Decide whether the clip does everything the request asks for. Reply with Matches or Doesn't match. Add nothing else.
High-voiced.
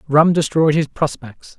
Doesn't match